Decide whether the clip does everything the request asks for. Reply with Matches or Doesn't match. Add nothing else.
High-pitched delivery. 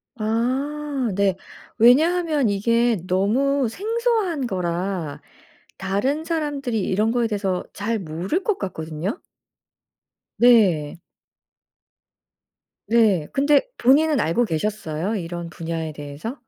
Matches